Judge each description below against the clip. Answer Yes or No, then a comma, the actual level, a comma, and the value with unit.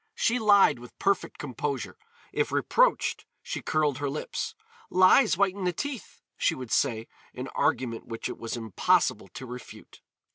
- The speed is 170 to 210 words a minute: No, average, 150 wpm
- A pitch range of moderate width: No, wide, 8.4 semitones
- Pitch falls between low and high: Yes, medium, 145 Hz